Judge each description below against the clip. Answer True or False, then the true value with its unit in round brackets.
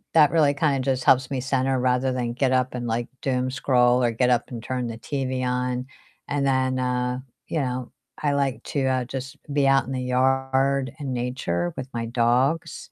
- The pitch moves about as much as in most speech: False (1.4 semitones)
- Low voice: True (130 Hz)